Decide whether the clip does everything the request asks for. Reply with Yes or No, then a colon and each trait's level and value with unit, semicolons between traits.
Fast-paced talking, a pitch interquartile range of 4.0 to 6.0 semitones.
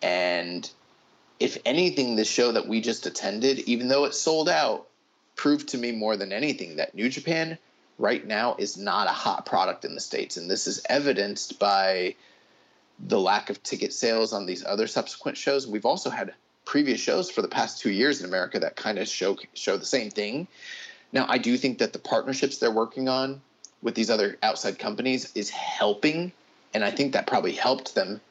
No: average, 195 wpm; average, 4.3 semitones